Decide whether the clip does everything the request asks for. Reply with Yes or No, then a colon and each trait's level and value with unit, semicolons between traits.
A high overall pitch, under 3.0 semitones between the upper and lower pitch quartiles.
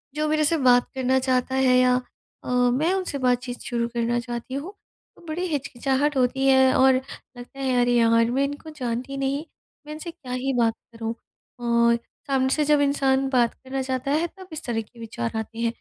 Yes: very high, 260 Hz; narrow, 2.6 semitones